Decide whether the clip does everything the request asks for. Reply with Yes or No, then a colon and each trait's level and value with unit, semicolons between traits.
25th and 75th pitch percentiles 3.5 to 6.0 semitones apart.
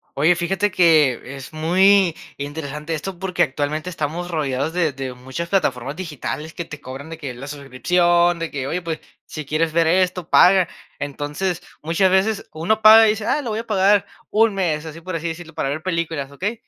Yes: average, 4.0 semitones